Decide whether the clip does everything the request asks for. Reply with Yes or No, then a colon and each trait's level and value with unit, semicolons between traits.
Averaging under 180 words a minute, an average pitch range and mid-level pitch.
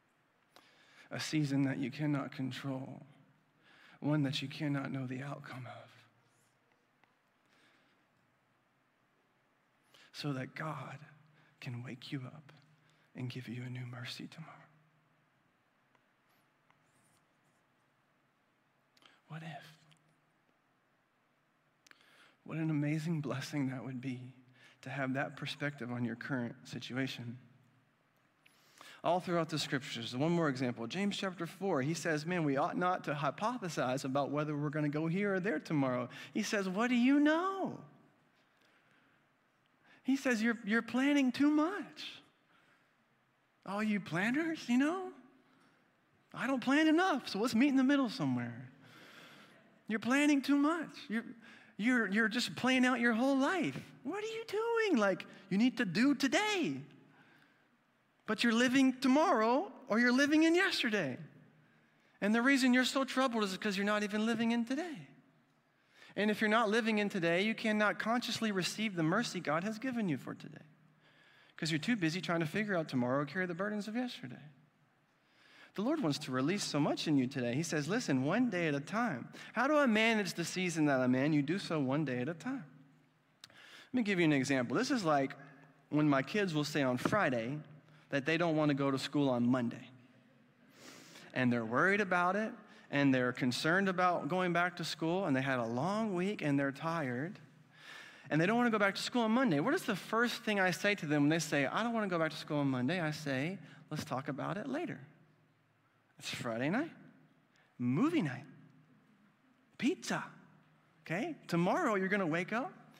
No: average, 170 wpm; wide, 8.3 semitones; medium, 165 Hz